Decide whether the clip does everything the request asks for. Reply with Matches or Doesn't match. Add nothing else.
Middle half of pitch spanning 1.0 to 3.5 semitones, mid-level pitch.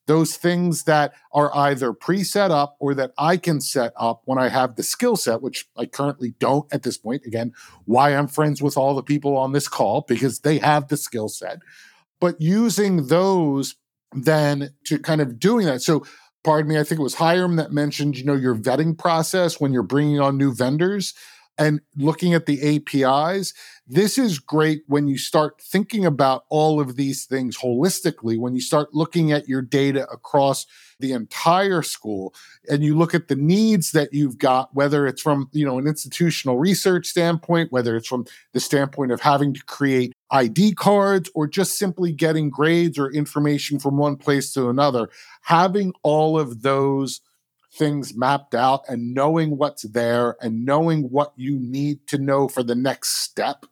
Matches